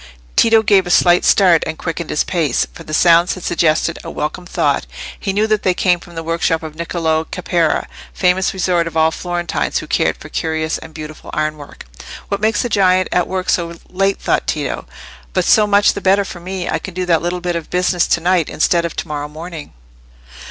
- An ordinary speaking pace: No, fast, 215 wpm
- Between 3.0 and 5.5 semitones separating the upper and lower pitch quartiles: No, narrow, 2.4 semitones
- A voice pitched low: No, medium, 175 Hz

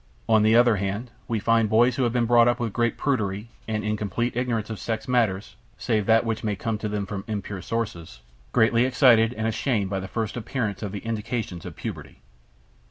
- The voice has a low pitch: Yes, low, 110 Hz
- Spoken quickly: Yes, fast, 210 wpm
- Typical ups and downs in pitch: No, narrow, 2.3 semitones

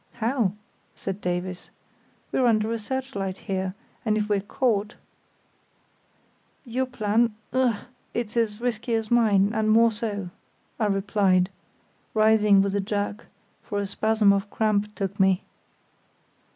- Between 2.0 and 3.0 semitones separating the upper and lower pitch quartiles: Yes, narrow, 2.5 semitones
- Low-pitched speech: No, high, 210 Hz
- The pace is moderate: No, slow, 125 wpm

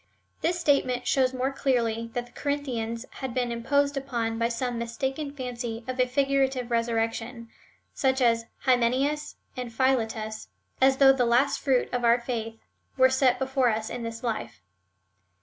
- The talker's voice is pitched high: Yes, very high, 250 Hz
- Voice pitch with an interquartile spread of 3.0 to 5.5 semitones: No, narrow, 2.4 semitones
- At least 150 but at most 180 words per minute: Yes, average, 160 wpm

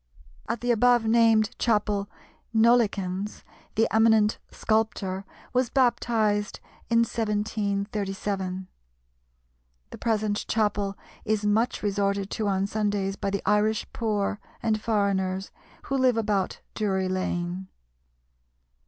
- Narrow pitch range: Yes, narrow, 2.0 semitones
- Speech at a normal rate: No, slow, 105 wpm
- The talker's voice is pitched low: No, high, 210 Hz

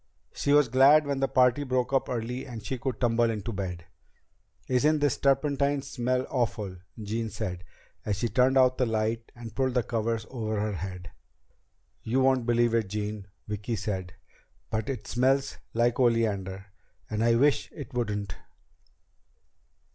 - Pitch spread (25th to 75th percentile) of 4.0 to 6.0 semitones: No, average, 3.5 semitones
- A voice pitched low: Yes, low, 115 Hz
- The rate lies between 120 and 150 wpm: No, average, 160 wpm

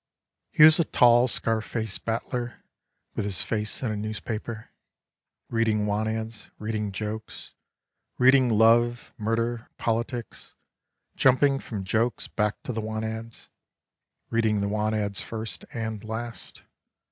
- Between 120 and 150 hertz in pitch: No, low, 110 Hz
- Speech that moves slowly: Yes, slow, 130 wpm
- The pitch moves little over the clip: Yes, narrow, 1.7 semitones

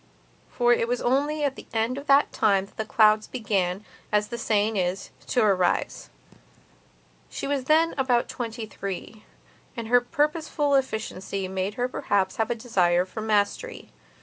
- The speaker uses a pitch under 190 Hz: No, high, 225 Hz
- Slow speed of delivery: No, average, 155 wpm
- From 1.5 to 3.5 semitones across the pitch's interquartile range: No, average, 4.2 semitones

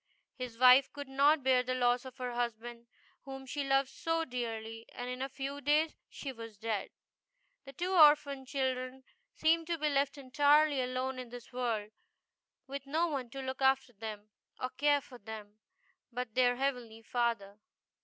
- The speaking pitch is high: Yes, very high, 255 Hz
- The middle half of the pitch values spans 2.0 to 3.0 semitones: Yes, narrow, 2.6 semitones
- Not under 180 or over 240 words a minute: No, average, 170 wpm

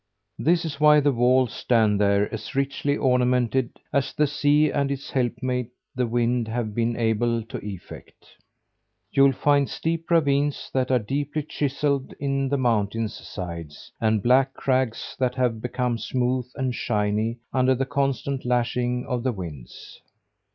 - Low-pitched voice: Yes, low, 125 Hz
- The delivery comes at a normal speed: Yes, average, 150 wpm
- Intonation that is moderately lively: Yes, average, 3.1 semitones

